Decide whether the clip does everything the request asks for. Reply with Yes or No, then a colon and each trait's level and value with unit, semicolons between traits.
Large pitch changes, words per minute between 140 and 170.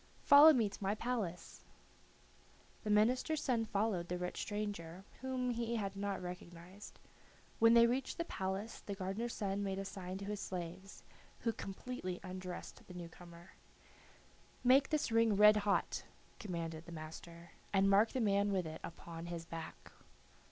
No: average, 4.0 semitones; average, 160 wpm